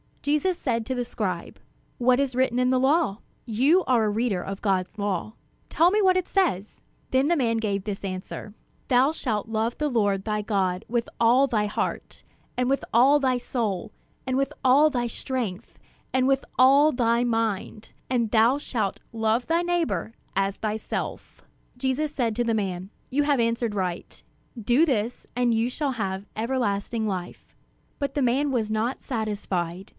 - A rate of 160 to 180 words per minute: Yes, average, 170 wpm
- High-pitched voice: Yes, high, 235 Hz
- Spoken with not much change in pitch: No, average, 4.0 semitones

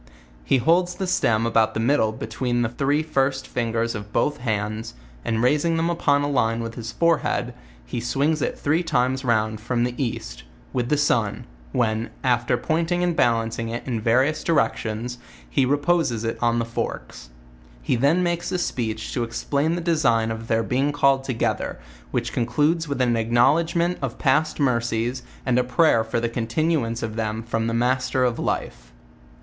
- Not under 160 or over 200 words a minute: Yes, average, 180 wpm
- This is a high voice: No, low, 125 Hz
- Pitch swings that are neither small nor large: Yes, average, 4.3 semitones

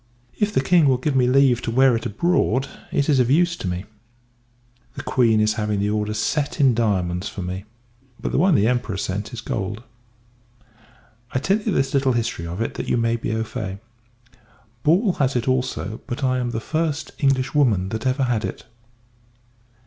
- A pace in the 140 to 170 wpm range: No, average, 195 wpm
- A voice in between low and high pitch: No, low, 125 Hz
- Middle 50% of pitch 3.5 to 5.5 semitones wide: Yes, average, 4.3 semitones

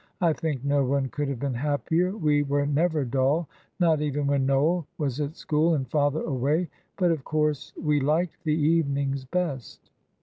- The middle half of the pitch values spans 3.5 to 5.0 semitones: No, narrow, 2.5 semitones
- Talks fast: No, average, 175 wpm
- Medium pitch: Yes, medium, 145 Hz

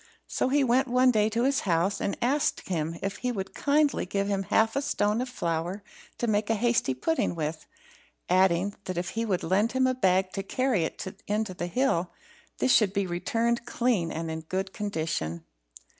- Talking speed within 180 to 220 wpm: Yes, average, 195 wpm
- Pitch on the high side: Yes, high, 200 Hz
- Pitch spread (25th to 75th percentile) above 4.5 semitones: Yes, average, 5.2 semitones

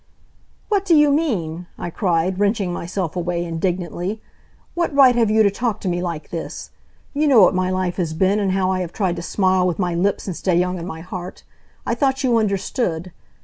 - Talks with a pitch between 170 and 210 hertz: Yes, medium, 185 Hz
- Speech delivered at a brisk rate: Yes, fast, 210 wpm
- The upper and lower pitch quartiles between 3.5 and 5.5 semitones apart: Yes, average, 3.8 semitones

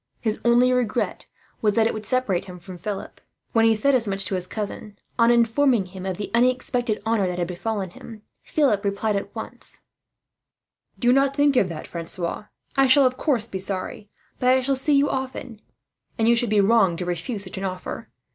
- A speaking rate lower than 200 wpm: No, fast, 205 wpm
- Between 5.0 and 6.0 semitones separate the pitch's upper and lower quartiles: No, average, 4.6 semitones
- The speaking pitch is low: No, high, 220 Hz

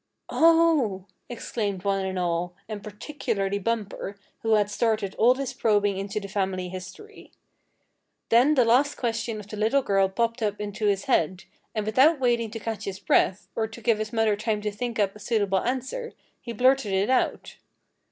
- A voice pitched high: Yes, high, 215 Hz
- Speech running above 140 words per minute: Yes, average, 180 wpm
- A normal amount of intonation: Yes, average, 3.2 semitones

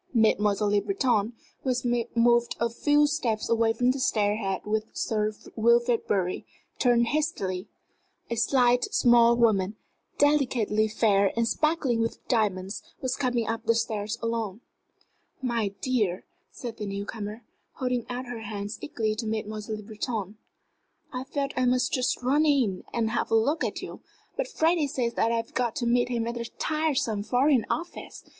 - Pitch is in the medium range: No, high, 235 Hz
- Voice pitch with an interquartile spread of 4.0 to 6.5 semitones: No, average, 2.8 semitones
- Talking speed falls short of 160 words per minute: No, average, 165 wpm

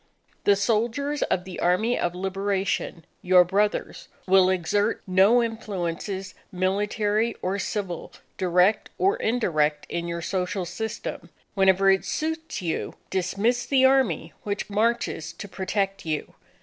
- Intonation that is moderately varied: Yes, average, 3.3 semitones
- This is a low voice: No, high, 195 Hz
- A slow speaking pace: Yes, slow, 125 wpm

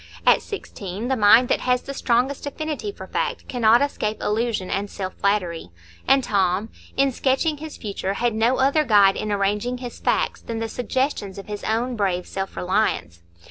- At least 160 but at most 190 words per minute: Yes, average, 180 wpm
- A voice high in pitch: Yes, high, 225 Hz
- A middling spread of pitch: Yes, average, 4.7 semitones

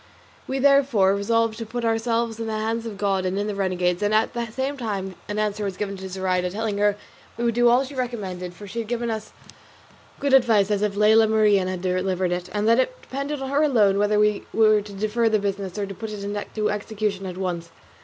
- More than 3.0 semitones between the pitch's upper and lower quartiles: No, average, 2.7 semitones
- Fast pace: Yes, fast, 235 wpm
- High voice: Yes, high, 210 Hz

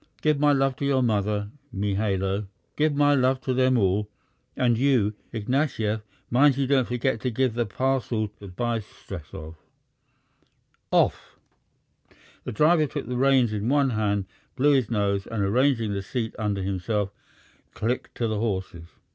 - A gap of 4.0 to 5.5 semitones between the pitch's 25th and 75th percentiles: Yes, average, 4.4 semitones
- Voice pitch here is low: Yes, low, 115 Hz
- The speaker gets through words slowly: No, average, 150 wpm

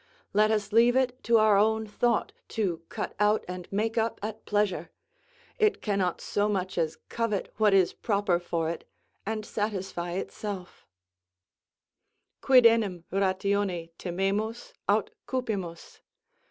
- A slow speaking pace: Yes, slow, 130 wpm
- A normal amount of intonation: Yes, average, 3.0 semitones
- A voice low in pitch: No, high, 205 Hz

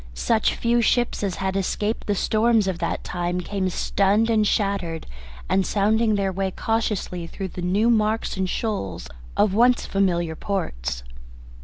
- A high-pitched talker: Yes, high, 195 Hz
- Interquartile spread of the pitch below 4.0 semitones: Yes, average, 3.2 semitones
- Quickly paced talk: No, average, 155 wpm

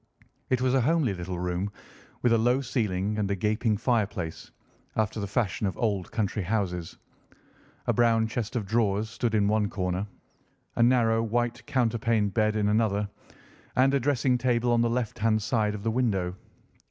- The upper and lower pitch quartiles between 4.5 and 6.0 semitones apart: No, average, 2.9 semitones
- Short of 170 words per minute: No, average, 175 wpm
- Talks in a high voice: No, low, 110 Hz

